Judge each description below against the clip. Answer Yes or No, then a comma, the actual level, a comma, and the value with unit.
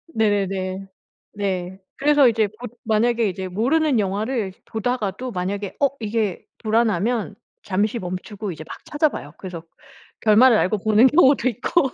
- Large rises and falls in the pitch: No, average, 4.0 semitones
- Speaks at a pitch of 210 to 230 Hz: Yes, high, 215 Hz